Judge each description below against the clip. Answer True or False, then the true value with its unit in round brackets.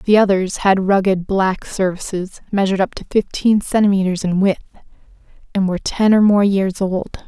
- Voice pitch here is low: False (195 Hz)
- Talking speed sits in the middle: True (165 wpm)